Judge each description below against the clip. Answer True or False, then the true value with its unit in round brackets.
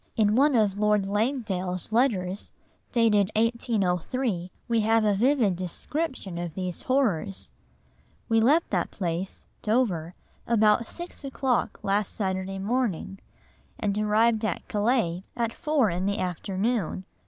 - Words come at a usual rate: False (125 wpm)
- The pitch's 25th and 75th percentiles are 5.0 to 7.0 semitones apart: False (3.8 semitones)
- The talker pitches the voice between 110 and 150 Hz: False (210 Hz)